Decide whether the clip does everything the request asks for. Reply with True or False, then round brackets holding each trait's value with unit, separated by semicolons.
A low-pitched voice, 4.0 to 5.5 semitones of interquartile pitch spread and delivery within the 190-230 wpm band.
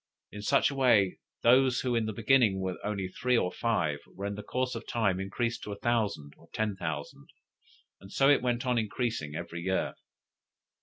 True (110 Hz; 4.4 semitones; 195 wpm)